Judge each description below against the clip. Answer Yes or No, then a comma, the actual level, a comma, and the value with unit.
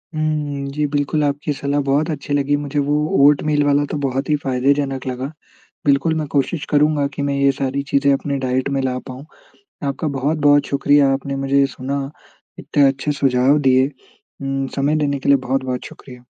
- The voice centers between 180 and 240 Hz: No, medium, 140 Hz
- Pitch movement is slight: Yes, narrow, 1.2 semitones